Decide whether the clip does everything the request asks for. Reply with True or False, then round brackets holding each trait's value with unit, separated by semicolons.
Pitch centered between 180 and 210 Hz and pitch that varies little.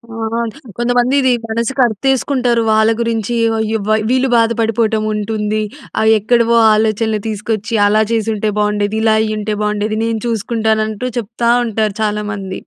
False (220 Hz; 1.6 semitones)